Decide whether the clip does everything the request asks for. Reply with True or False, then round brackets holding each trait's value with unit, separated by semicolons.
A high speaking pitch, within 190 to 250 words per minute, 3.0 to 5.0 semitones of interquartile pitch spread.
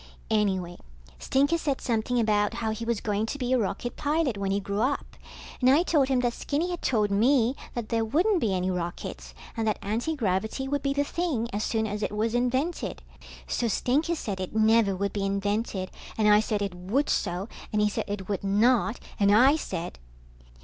True (220 Hz; 200 wpm; 4.6 semitones)